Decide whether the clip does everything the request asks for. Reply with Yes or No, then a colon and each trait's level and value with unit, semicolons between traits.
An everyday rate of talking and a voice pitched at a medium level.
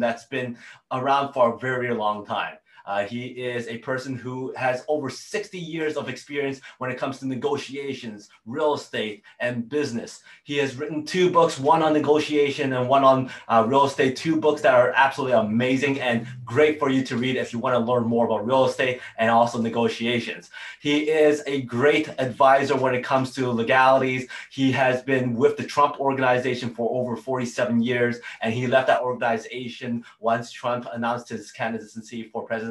No: average, 185 wpm; low, 130 Hz